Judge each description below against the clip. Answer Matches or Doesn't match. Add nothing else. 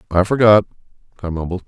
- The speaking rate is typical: Matches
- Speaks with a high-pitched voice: Doesn't match